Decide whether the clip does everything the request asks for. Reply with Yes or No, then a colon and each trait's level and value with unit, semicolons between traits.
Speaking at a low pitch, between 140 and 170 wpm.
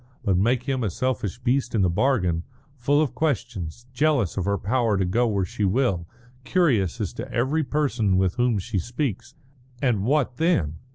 No: low, 120 Hz; average, 180 wpm